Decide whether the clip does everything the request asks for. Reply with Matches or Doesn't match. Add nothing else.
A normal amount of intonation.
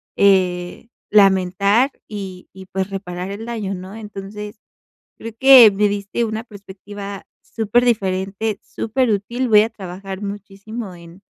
Doesn't match